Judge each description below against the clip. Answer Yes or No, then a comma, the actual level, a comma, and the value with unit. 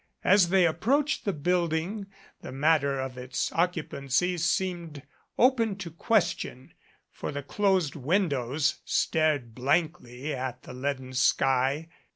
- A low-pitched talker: No, medium, 155 Hz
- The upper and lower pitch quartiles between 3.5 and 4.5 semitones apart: No, average, 5.2 semitones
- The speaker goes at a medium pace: No, slow, 125 wpm